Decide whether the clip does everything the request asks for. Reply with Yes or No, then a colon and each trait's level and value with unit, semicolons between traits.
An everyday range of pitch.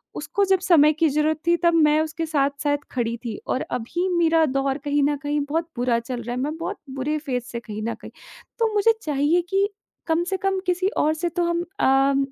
Yes: average, 4.0 semitones